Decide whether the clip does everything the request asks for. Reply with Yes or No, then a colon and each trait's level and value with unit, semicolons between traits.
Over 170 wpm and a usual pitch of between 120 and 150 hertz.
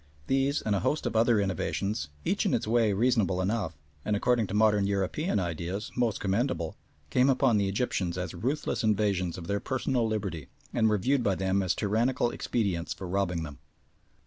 No: average, 180 wpm; low, 100 Hz